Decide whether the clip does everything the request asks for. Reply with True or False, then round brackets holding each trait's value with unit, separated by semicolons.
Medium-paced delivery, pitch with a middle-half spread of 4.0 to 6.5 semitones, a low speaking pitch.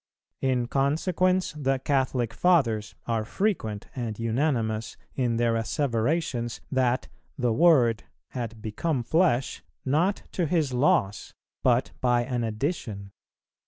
False (115 wpm; 4.6 semitones; 125 Hz)